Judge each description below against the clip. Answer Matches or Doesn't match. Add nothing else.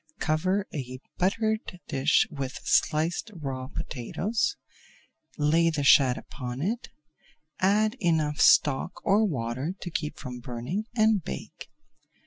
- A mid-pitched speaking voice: Matches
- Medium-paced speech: Doesn't match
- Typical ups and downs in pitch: Doesn't match